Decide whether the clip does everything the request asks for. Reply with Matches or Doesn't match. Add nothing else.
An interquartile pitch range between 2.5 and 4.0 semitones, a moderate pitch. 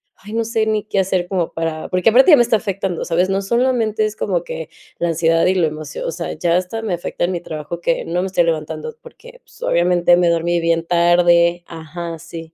Matches